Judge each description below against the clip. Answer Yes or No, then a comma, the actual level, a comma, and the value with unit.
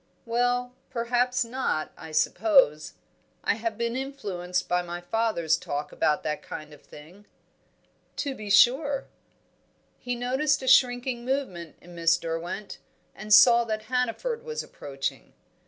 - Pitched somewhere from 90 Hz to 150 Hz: No, high, 230 Hz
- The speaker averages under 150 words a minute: Yes, slow, 135 wpm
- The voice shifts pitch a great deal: Yes, wide, 6.5 semitones